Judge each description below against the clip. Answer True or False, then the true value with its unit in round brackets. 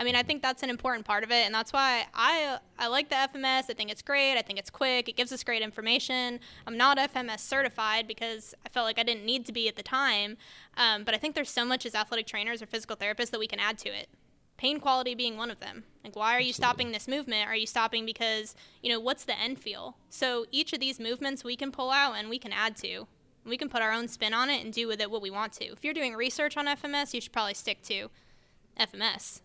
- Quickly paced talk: True (270 wpm)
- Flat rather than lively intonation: False (3.0 semitones)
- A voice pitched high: True (240 Hz)